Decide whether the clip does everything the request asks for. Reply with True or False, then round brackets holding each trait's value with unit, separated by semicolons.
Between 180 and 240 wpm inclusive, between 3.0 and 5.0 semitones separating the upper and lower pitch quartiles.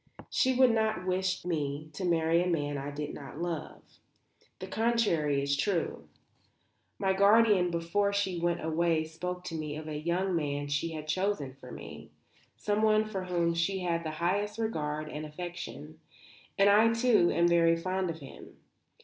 False (165 wpm; 4.1 semitones)